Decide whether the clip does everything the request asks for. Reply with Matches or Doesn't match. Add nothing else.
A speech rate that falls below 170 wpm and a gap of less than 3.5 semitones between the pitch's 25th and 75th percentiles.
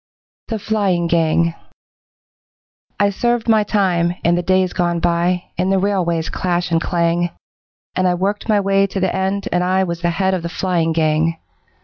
Doesn't match